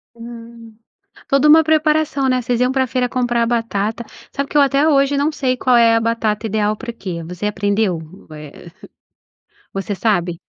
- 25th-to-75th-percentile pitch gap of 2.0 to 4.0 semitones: No, average, 4.5 semitones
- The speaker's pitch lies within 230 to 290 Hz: Yes, high, 235 Hz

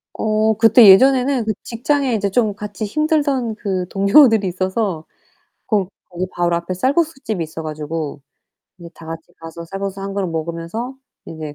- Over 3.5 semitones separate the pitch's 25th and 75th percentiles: Yes, average, 5.3 semitones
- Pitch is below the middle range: No, high, 195 Hz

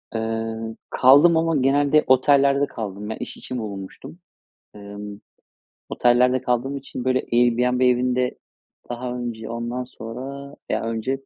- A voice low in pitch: Yes, low, 125 Hz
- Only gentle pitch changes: No, average, 3.1 semitones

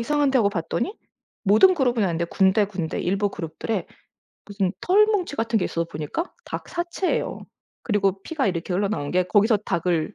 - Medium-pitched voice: No, high, 205 Hz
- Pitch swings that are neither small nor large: No, wide, 6.4 semitones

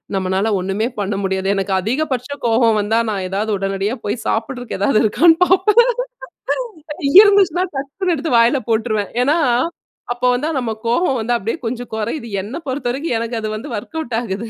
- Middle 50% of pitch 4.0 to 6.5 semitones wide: Yes, average, 5.1 semitones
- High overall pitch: Yes, high, 230 Hz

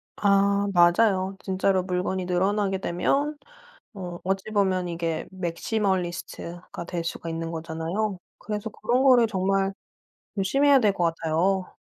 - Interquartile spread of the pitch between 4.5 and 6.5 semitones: No, average, 2.8 semitones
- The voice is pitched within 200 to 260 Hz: No, high, 190 Hz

